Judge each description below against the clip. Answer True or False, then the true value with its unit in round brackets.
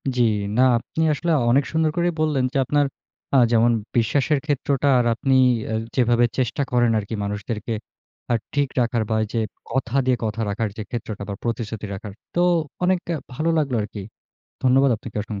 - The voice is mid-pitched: False (125 Hz)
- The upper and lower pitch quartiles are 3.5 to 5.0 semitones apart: True (4.1 semitones)